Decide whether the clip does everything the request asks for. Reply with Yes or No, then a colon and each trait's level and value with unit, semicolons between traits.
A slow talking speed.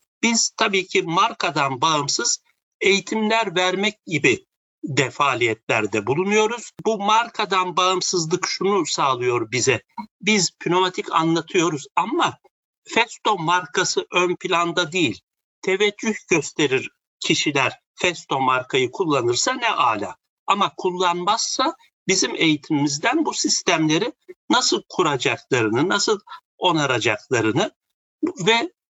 Yes: slow, 90 wpm